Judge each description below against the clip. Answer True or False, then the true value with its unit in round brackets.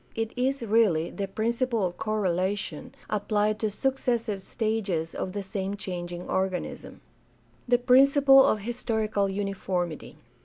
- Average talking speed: False (120 wpm)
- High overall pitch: True (210 Hz)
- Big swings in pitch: False (3.6 semitones)